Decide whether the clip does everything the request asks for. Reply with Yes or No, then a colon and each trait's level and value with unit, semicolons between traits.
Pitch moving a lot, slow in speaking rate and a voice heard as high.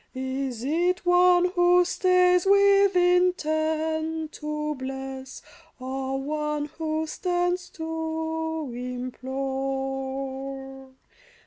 No: average, 4.8 semitones; slow, 80 wpm; very high, 310 Hz